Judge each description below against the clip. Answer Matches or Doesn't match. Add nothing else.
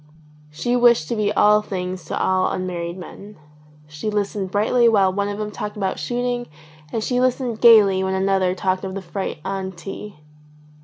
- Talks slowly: Doesn't match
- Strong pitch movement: Doesn't match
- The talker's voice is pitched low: Doesn't match